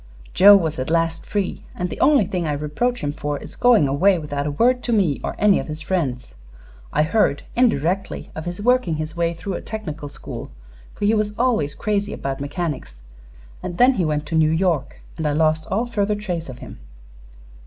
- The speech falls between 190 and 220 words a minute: Yes, fast, 205 wpm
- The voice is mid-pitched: Yes, medium, 170 Hz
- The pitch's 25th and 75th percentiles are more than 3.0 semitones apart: Yes, wide, 5.6 semitones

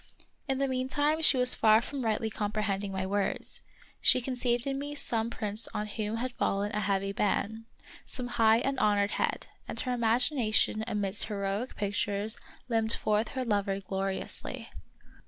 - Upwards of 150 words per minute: Yes, average, 165 wpm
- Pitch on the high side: Yes, high, 220 Hz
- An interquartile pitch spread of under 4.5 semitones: Yes, average, 3.5 semitones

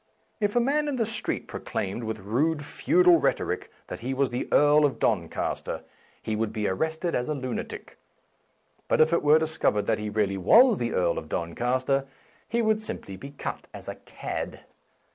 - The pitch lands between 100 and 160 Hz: Yes, low, 135 Hz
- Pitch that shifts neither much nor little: No, wide, 7.8 semitones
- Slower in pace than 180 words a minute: No, average, 195 wpm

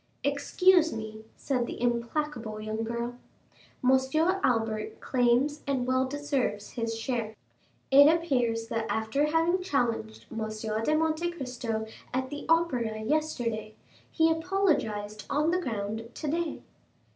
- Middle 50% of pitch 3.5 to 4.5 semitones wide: No, wide, 5.5 semitones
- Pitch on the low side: No, very high, 255 Hz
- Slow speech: Yes, slow, 120 wpm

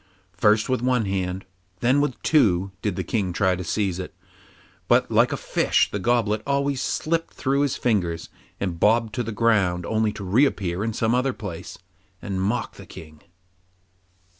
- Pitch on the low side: Yes, low, 105 Hz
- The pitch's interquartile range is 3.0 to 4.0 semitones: No, average, 4.7 semitones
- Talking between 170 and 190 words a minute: Yes, average, 175 wpm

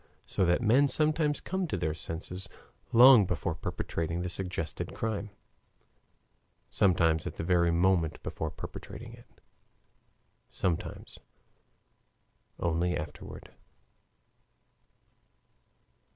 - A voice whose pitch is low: Yes, very low, 90 Hz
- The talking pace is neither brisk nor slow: No, slow, 95 wpm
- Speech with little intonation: No, average, 4.9 semitones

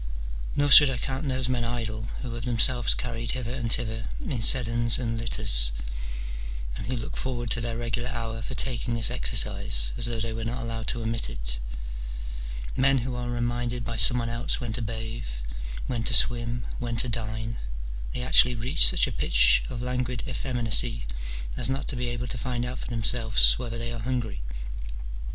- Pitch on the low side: Yes, low, 120 Hz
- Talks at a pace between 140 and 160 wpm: No, average, 190 wpm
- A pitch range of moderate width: No, narrow, 1.6 semitones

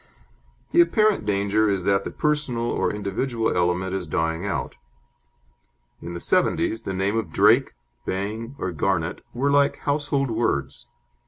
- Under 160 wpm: Yes, average, 145 wpm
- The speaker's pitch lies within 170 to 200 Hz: No, low, 105 Hz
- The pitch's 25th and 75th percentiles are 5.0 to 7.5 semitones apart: Yes, wide, 5.6 semitones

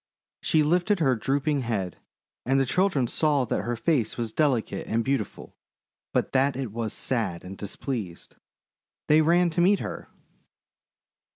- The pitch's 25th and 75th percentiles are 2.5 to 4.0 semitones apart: No, average, 5.2 semitones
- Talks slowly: No, average, 150 wpm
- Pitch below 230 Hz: Yes, low, 135 Hz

